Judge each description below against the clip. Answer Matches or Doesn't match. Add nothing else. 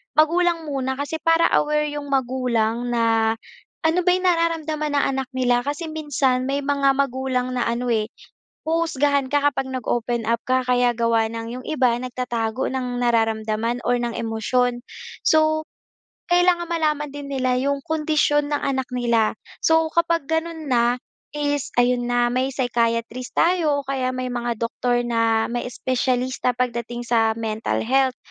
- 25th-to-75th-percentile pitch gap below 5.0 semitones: Matches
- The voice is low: Doesn't match